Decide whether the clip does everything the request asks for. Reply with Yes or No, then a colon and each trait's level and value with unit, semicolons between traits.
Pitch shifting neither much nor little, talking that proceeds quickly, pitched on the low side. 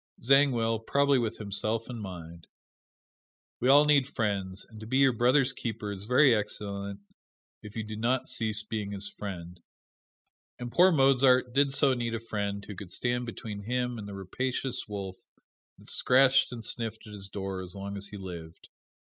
No: average, 4.0 semitones; average, 175 wpm; low, 110 Hz